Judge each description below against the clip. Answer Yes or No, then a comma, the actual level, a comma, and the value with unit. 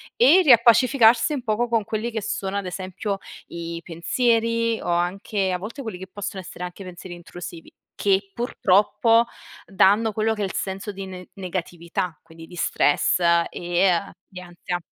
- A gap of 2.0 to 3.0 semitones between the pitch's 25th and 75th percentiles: No, average, 4.0 semitones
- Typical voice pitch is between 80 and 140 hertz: No, high, 195 Hz